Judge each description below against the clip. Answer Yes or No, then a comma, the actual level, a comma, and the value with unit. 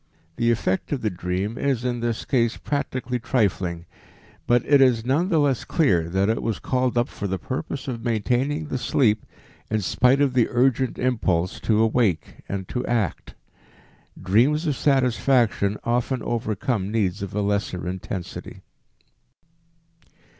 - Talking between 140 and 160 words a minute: Yes, average, 150 wpm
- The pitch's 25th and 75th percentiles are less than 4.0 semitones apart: No, average, 4.3 semitones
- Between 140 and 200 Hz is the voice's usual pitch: No, low, 115 Hz